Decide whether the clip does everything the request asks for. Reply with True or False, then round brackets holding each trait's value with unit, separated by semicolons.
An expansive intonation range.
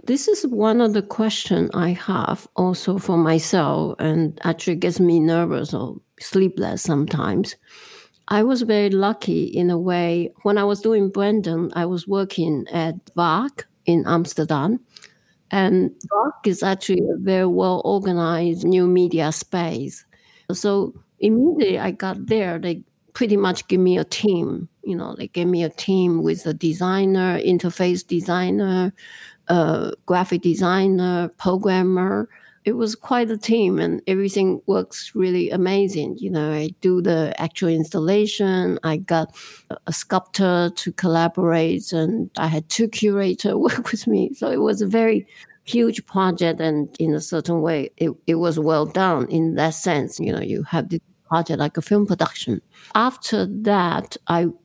False (3.4 semitones)